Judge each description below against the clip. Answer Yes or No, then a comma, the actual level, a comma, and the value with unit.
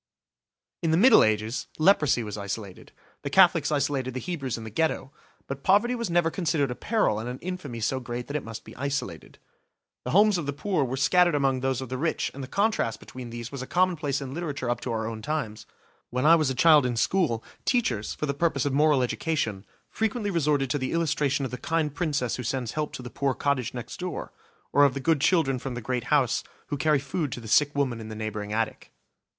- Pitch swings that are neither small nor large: Yes, average, 4.7 semitones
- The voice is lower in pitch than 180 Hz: Yes, medium, 140 Hz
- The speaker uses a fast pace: Yes, fast, 230 wpm